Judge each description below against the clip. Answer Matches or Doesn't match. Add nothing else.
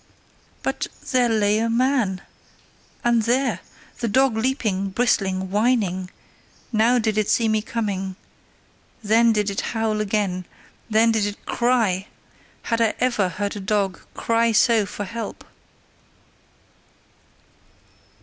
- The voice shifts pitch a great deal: Doesn't match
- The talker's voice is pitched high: Matches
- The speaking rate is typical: Doesn't match